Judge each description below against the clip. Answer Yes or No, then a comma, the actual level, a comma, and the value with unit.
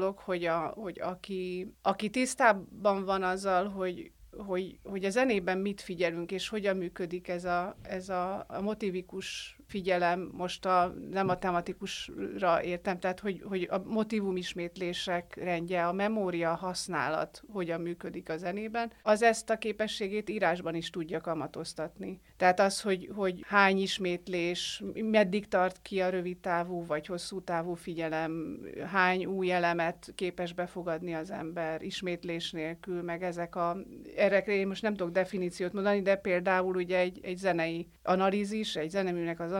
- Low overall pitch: No, medium, 185 Hz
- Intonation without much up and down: Yes, narrow, 2.1 semitones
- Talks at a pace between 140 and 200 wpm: Yes, average, 150 wpm